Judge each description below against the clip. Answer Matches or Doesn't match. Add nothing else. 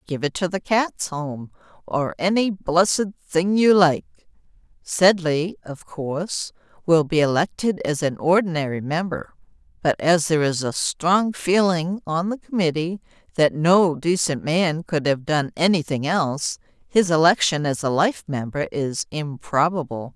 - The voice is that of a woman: Matches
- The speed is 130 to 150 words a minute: Matches